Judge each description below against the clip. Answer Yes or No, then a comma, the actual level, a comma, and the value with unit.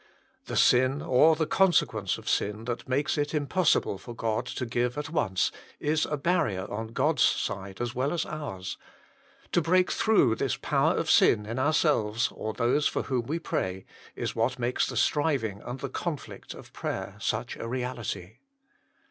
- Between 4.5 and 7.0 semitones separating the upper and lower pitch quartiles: Yes, average, 5.3 semitones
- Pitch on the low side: Yes, low, 125 Hz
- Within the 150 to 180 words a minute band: Yes, average, 175 wpm